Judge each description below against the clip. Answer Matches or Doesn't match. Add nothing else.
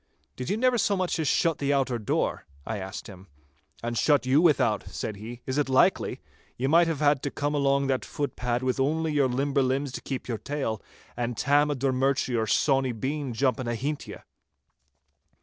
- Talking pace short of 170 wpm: Doesn't match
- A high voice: Doesn't match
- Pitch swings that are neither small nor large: Matches